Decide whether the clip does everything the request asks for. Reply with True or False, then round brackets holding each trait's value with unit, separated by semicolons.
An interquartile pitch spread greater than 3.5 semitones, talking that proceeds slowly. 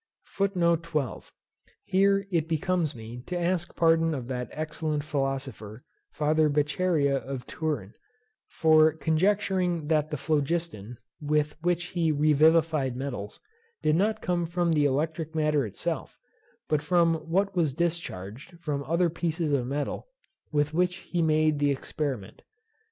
False (3.1 semitones; 130 wpm)